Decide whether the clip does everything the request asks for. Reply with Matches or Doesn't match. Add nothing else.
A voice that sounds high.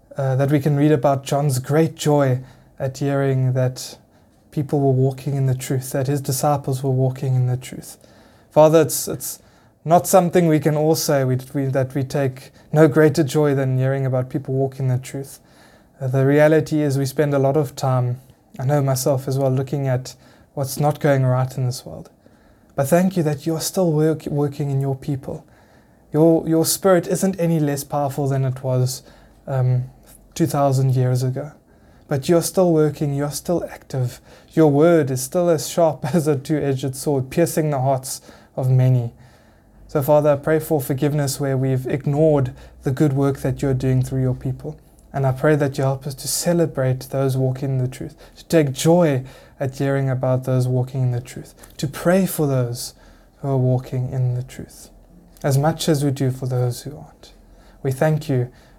Doesn't match